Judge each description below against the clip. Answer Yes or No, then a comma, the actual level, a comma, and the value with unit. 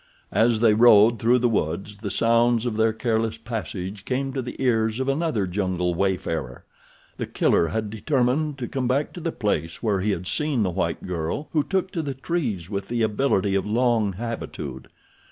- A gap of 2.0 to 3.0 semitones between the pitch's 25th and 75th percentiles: No, average, 4.4 semitones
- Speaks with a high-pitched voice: No, low, 110 Hz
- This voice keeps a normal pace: Yes, average, 190 wpm